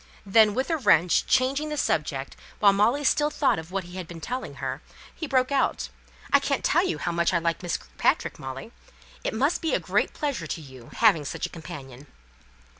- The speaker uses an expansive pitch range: Yes, wide, 8.4 semitones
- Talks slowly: No, fast, 205 wpm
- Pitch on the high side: Yes, high, 195 Hz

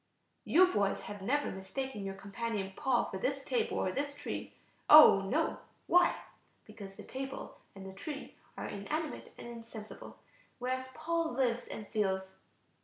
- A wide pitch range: Yes, wide, 6.3 semitones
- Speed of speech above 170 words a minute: No, average, 155 wpm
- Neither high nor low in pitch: No, high, 240 Hz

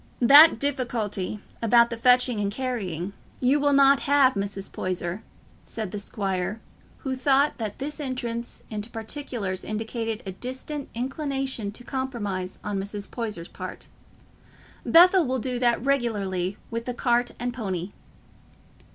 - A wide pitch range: No, average, 4.5 semitones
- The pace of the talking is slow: Yes, slow, 130 wpm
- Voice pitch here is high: Yes, high, 235 Hz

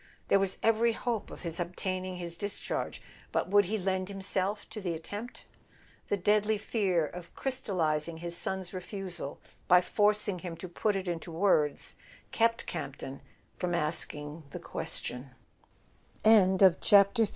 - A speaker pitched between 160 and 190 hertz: Yes, medium, 185 Hz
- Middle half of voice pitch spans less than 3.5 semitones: Yes, average, 3.1 semitones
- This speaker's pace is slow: Yes, slow, 130 wpm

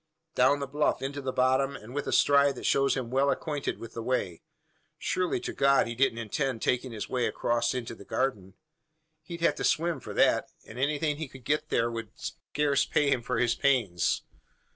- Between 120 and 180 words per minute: No, fast, 205 wpm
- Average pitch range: Yes, average, 3.2 semitones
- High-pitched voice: No, low, 130 Hz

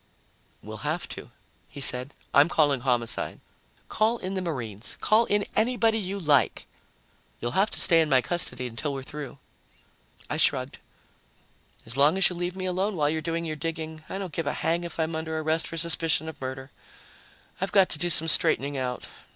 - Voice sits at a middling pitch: Yes, medium, 160 Hz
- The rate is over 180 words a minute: Yes, average, 190 wpm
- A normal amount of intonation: Yes, average, 4.5 semitones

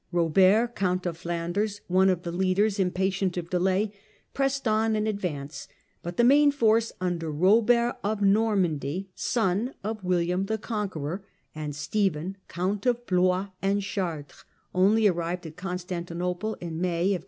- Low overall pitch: No, medium, 185 Hz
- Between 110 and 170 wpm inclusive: Yes, average, 150 wpm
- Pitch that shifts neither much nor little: Yes, average, 3.5 semitones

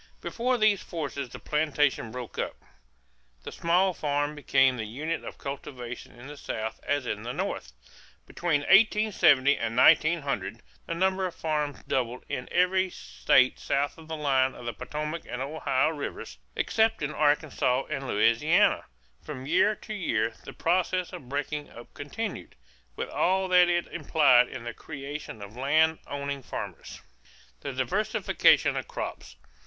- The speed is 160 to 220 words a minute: No, average, 150 wpm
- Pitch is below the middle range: No, medium, 145 Hz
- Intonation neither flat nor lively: Yes, average, 4.7 semitones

